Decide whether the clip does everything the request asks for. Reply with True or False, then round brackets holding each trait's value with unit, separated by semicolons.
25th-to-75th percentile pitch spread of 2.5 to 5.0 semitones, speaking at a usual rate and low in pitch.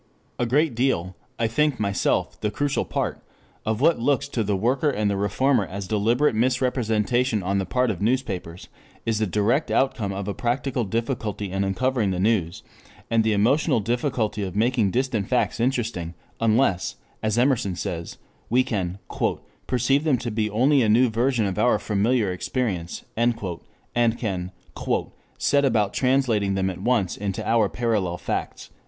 True (4.2 semitones; 160 wpm; 110 Hz)